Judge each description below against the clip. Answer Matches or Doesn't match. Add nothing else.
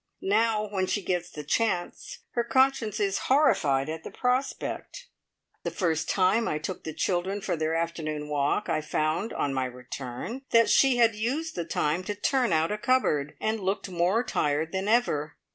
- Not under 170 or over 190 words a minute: Matches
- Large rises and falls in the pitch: Matches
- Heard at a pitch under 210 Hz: Matches